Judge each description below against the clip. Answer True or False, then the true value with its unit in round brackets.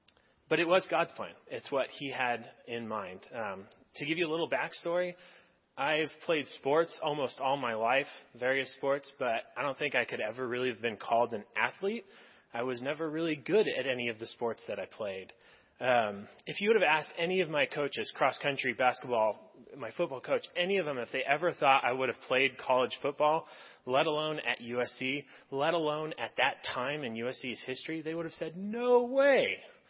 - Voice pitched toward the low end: False (145 Hz)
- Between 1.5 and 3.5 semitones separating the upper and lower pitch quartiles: False (4.9 semitones)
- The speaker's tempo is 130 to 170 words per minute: False (195 wpm)